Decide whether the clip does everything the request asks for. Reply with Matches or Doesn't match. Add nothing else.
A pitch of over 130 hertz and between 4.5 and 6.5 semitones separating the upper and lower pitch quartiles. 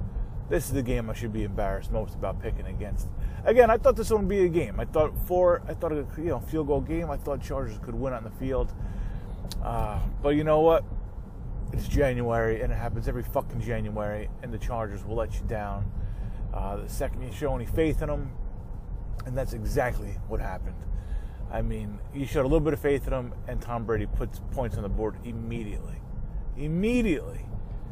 Doesn't match